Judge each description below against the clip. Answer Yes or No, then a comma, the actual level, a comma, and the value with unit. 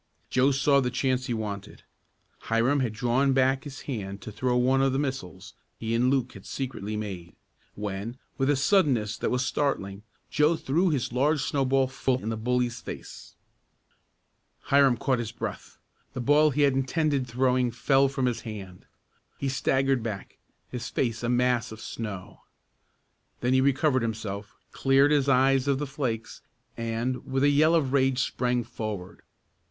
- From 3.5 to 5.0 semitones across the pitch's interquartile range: No, average, 3.1 semitones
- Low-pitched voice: Yes, low, 130 Hz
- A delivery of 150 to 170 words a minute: Yes, average, 165 wpm